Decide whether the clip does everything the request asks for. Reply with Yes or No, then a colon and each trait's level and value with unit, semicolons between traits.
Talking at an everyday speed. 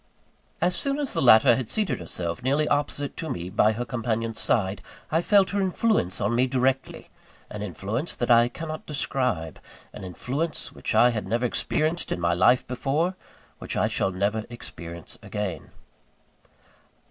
Yes: average, 160 wpm